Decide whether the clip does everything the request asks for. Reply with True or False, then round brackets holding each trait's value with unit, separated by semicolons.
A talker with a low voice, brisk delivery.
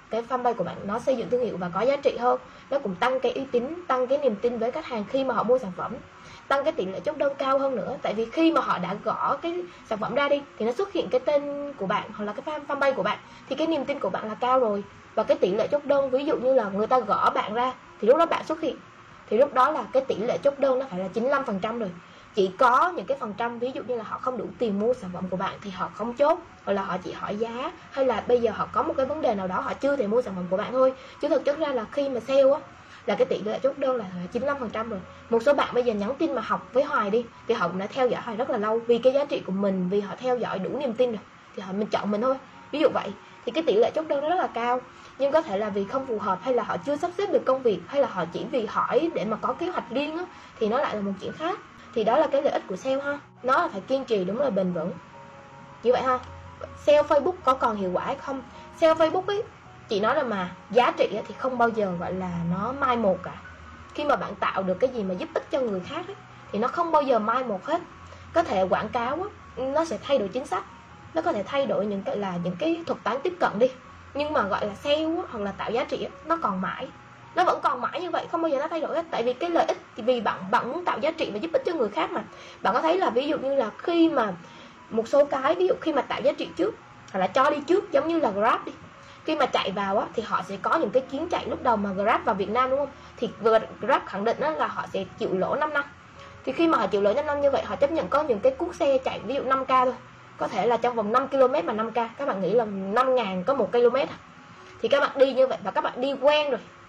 False (255 Hz; 300 wpm)